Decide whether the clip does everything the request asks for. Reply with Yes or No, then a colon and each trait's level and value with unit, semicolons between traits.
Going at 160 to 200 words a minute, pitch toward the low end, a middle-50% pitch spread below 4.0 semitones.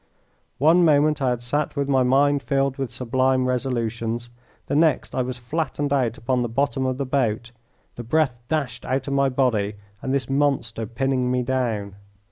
Yes: average, 180 wpm; low, 130 Hz; narrow, 2.5 semitones